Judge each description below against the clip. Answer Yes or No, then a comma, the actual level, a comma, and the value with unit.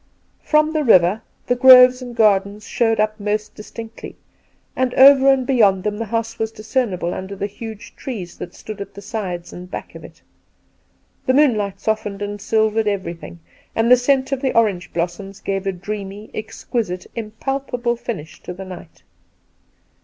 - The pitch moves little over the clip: No, average, 3.8 semitones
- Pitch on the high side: Yes, high, 215 Hz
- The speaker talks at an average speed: Yes, average, 165 wpm